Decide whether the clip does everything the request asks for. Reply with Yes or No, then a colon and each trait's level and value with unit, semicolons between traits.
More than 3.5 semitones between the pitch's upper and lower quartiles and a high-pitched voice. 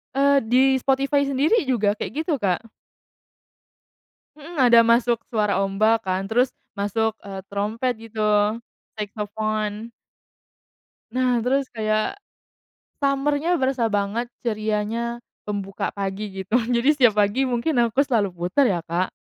Yes: average, 4.2 semitones; high, 230 Hz